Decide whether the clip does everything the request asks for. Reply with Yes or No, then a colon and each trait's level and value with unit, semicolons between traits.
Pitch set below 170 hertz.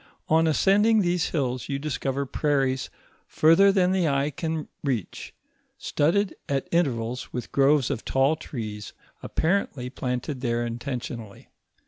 Yes: medium, 140 Hz